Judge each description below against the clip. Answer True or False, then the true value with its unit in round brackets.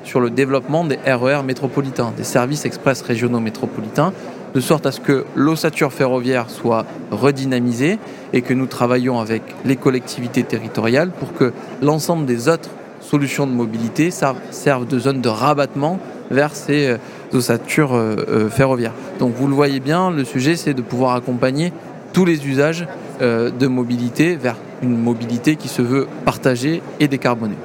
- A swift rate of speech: False (160 wpm)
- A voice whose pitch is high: False (135 Hz)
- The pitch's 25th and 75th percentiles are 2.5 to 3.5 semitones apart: True (3.0 semitones)